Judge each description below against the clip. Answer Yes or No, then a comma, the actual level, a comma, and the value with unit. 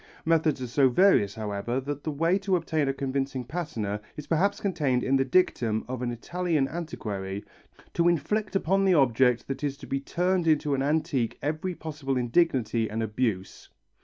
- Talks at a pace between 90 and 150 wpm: No, average, 175 wpm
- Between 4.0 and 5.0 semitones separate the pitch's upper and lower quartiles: No, wide, 5.4 semitones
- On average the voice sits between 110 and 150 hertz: Yes, medium, 140 Hz